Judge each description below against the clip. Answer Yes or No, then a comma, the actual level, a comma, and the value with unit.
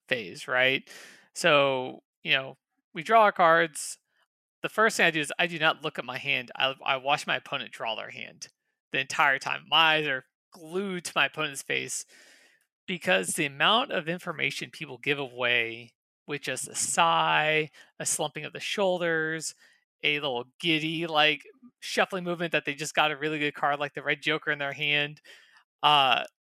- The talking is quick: No, average, 180 wpm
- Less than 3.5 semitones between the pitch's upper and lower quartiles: Yes, average, 3.0 semitones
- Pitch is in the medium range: Yes, medium, 155 Hz